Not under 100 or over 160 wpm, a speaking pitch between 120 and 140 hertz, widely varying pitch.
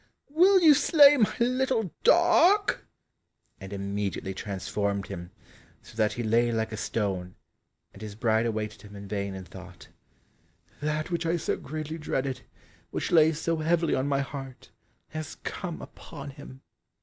Yes: average, 150 wpm; low, 135 Hz; wide, 8.2 semitones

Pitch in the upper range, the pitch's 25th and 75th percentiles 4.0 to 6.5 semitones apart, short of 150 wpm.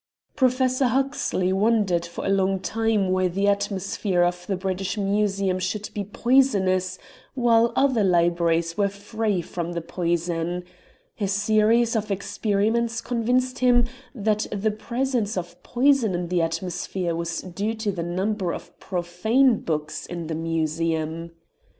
Yes: high, 195 Hz; average, 4.3 semitones; average, 140 wpm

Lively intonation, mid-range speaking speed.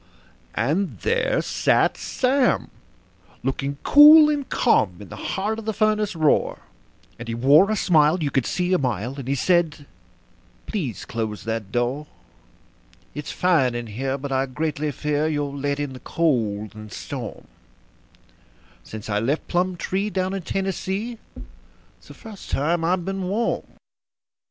Yes: wide, 6.9 semitones; average, 150 wpm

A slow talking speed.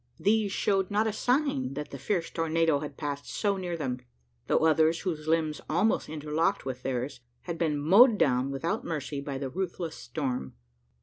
No: average, 175 wpm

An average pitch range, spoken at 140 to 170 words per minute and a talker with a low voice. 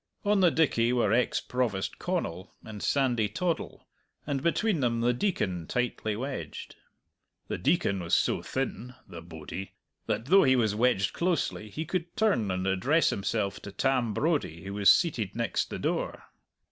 No: wide, 7.0 semitones; average, 160 wpm; low, 120 Hz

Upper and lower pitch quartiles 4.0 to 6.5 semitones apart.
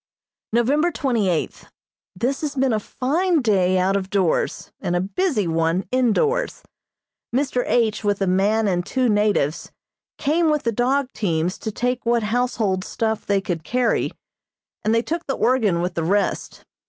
Yes: wide, 5.4 semitones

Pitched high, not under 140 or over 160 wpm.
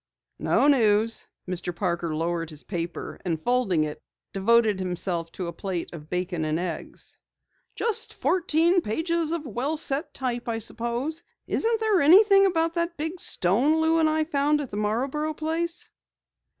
Yes: high, 245 Hz; average, 155 wpm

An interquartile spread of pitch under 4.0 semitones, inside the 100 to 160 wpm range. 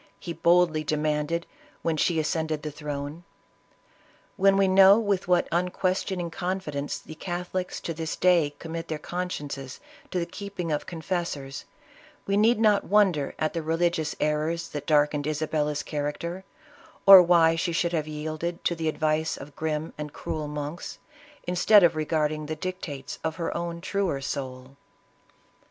Yes: average, 2.9 semitones; average, 150 wpm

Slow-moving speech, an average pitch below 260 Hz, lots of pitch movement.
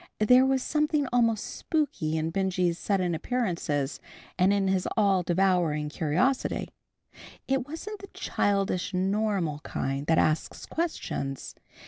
Yes: slow, 120 wpm; high, 190 Hz; wide, 7.3 semitones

